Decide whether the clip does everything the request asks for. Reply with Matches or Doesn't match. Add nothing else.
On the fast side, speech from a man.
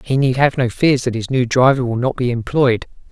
Matches